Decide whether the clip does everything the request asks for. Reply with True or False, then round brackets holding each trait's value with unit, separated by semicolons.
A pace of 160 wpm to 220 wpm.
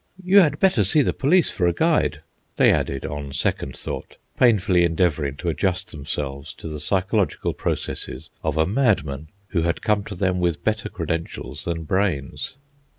True (165 wpm)